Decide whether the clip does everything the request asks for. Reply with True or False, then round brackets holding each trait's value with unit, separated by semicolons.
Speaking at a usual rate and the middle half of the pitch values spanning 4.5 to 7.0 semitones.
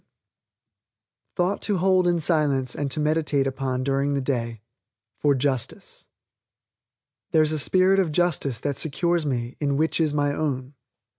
False (145 wpm; 3.2 semitones)